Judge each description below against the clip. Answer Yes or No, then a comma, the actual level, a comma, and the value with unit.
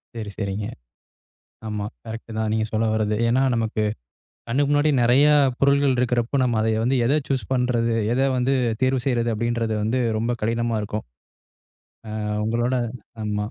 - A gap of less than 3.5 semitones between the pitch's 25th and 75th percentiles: Yes, average, 2.9 semitones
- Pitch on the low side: Yes, low, 115 Hz